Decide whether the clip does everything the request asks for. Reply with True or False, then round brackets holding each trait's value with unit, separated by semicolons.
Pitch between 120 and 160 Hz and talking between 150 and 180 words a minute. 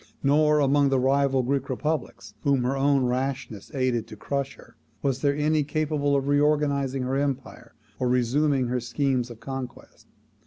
True (135 Hz; 160 wpm)